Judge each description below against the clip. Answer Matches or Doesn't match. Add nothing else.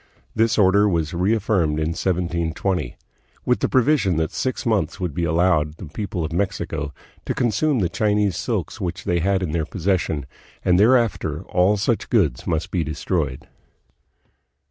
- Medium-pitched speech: Doesn't match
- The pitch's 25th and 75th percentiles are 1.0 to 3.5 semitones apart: Doesn't match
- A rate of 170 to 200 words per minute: Doesn't match